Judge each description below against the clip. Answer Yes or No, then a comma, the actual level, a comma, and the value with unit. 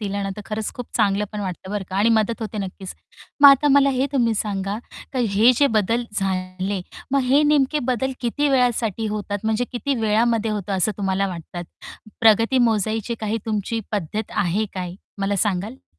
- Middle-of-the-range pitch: No, high, 215 Hz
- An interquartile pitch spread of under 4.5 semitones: Yes, average, 3.4 semitones